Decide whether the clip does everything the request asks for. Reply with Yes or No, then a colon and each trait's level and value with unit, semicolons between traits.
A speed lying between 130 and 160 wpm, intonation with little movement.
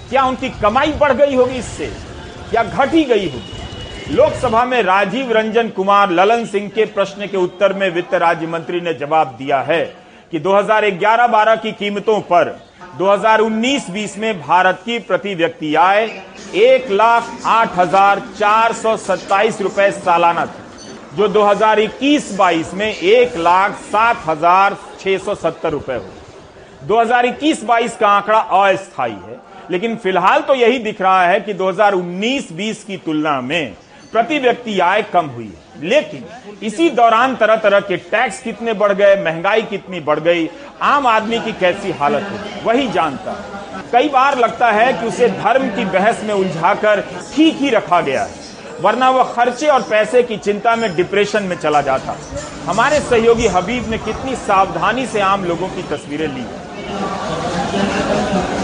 No: average, 155 wpm; average, 3.9 semitones